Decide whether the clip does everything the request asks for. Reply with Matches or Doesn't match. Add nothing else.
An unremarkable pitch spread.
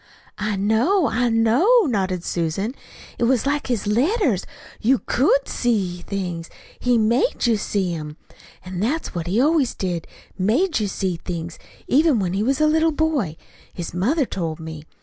Doesn't match